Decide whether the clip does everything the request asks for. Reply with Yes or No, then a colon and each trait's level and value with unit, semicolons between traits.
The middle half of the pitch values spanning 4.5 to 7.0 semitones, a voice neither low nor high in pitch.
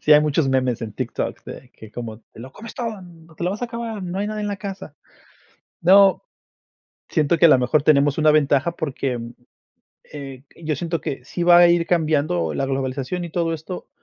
Yes: average, 4.9 semitones; medium, 155 Hz